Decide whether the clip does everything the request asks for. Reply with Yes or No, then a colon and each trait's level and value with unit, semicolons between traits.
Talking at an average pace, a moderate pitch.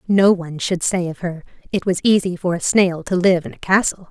No: fast, 250 wpm; medium, 180 Hz